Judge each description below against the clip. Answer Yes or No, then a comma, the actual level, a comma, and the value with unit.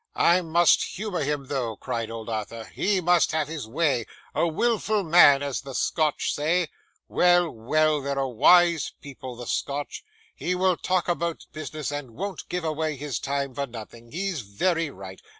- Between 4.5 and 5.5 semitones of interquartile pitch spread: Yes, average, 5.0 semitones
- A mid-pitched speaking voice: Yes, medium, 150 Hz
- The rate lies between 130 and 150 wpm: No, average, 170 wpm